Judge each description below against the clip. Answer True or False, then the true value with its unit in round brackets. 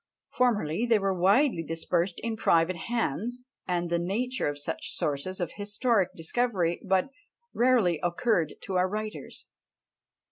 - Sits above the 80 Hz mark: True (190 Hz)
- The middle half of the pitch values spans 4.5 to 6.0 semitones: True (5.3 semitones)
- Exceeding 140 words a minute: False (135 wpm)